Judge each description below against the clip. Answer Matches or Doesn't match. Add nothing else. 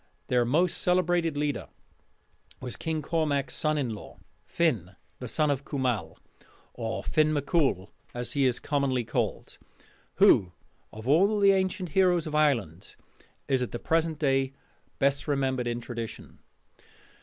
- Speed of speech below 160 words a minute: Matches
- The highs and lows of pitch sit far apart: Doesn't match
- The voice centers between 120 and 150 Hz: Matches